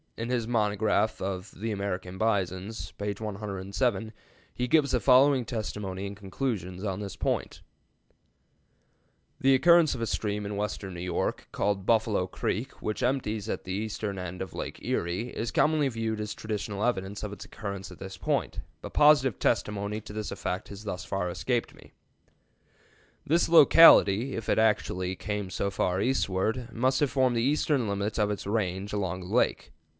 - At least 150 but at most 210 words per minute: Yes, average, 170 wpm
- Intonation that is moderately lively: Yes, average, 3.4 semitones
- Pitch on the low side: Yes, low, 105 Hz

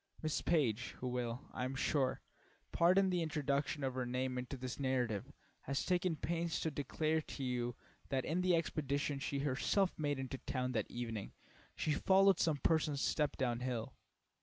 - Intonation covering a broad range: No, average, 3.9 semitones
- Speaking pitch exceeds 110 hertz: Yes, medium, 140 Hz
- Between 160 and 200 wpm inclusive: Yes, average, 170 wpm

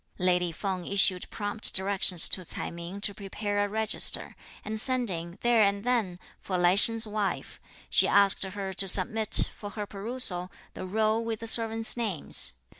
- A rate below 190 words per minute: Yes, average, 165 wpm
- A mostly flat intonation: No, average, 3.0 semitones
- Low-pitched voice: No, high, 200 Hz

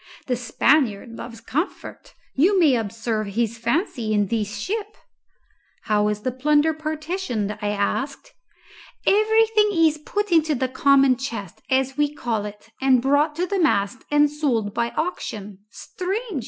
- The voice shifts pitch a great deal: Yes, wide, 6.0 semitones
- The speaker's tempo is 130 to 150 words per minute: Yes, average, 145 wpm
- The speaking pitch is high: Yes, very high, 265 Hz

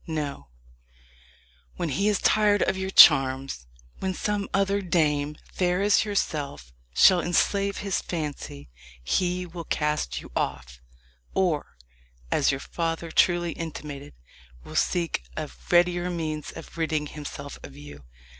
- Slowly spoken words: Yes, slow, 130 wpm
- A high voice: No, medium, 165 Hz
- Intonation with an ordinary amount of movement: Yes, average, 4.2 semitones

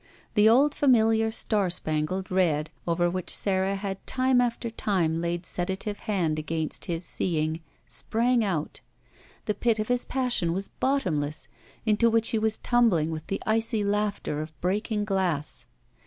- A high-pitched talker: Yes, high, 195 Hz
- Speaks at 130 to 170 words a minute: Yes, average, 150 wpm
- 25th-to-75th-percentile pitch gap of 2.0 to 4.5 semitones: No, average, 4.9 semitones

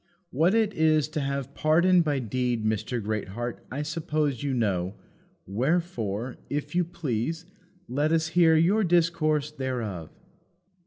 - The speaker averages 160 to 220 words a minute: No, slow, 135 wpm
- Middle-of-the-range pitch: Yes, medium, 145 Hz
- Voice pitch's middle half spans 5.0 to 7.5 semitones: Yes, average, 5.3 semitones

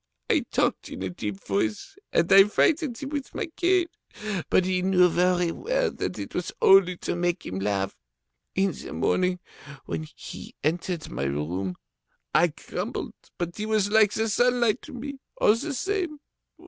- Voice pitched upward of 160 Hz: Yes, medium, 185 Hz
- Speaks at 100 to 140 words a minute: No, average, 170 wpm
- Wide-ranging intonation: Yes, wide, 7.6 semitones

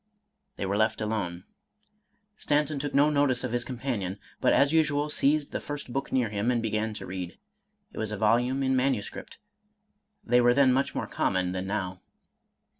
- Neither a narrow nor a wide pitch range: Yes, average, 4.9 semitones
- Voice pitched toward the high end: No, low, 120 Hz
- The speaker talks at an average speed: Yes, average, 190 wpm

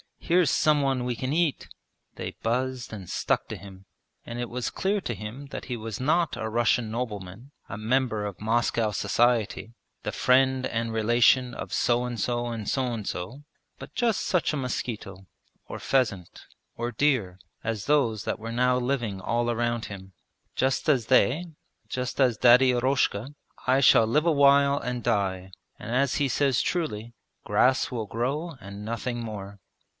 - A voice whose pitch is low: Yes, low, 120 Hz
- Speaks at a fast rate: No, average, 170 wpm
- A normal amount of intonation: Yes, average, 3.3 semitones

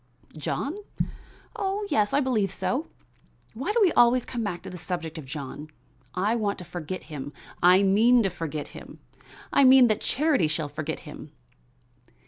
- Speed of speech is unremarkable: Yes, average, 165 wpm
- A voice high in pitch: Yes, high, 195 Hz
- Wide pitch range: Yes, wide, 7.8 semitones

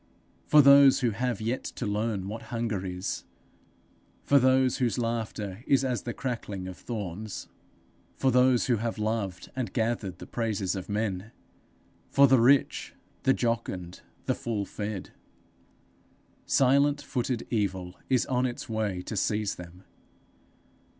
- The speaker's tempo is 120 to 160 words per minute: Yes, average, 140 wpm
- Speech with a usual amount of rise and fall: Yes, average, 4.0 semitones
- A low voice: Yes, low, 115 Hz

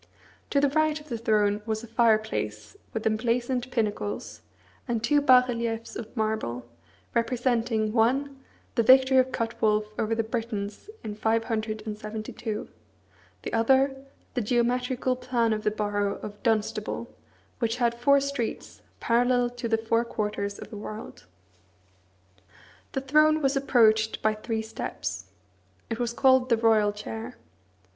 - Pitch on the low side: No, high, 230 Hz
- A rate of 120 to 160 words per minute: Yes, slow, 135 wpm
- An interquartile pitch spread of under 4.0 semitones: Yes, narrow, 2.6 semitones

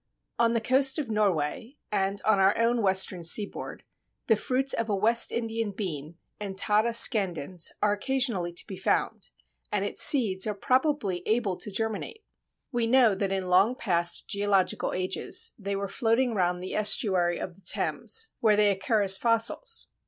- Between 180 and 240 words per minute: No, average, 165 wpm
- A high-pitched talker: Yes, high, 210 Hz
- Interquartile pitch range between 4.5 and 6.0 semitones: No, average, 3.4 semitones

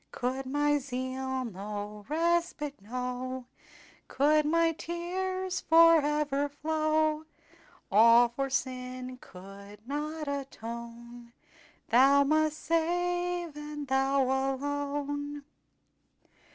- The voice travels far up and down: No, average, 3.6 semitones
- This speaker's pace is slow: Yes, slow, 85 wpm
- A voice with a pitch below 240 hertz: No, very high, 280 Hz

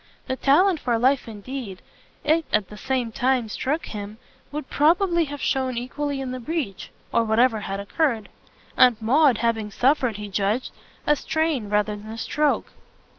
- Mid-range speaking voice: No, very high, 250 Hz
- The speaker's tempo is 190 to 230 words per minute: No, average, 165 wpm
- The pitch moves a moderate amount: Yes, average, 5.0 semitones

